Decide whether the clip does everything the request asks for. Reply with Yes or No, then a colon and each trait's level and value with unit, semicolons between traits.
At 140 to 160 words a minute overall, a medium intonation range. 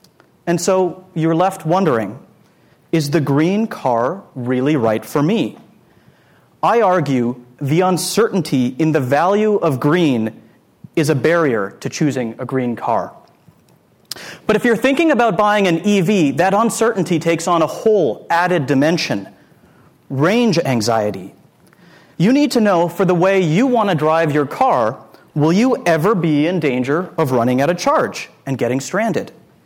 No: average, 150 wpm; wide, 6.0 semitones